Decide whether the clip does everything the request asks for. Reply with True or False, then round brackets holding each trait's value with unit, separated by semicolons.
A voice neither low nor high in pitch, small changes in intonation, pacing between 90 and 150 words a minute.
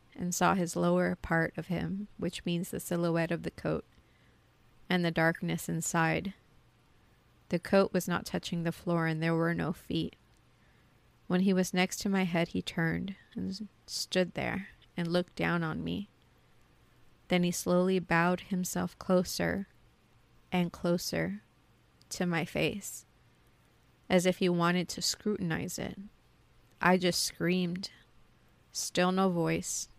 True (175 Hz; 2.0 semitones; 140 wpm)